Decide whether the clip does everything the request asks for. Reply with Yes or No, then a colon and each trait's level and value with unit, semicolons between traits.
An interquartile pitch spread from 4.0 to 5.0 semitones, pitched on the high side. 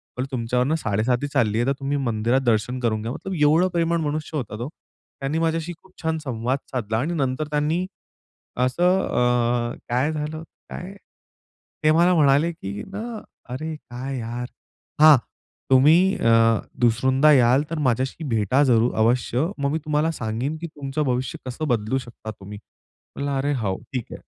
No: average, 4.4 semitones; low, 135 Hz